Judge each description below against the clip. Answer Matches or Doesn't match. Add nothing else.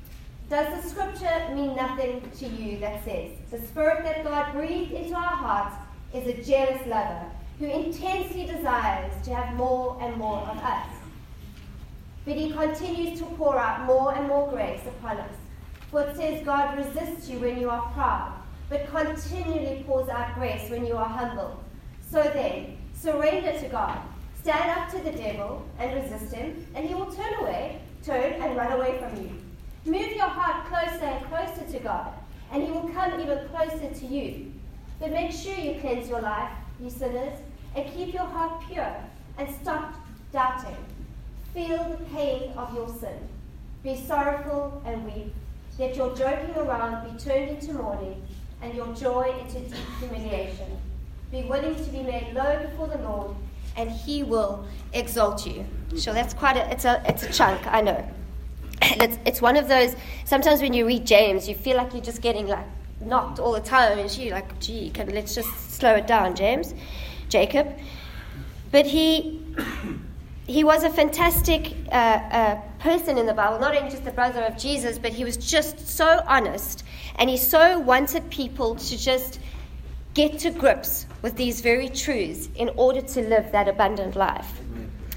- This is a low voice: Doesn't match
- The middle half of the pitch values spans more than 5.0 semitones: Doesn't match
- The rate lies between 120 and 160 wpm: Doesn't match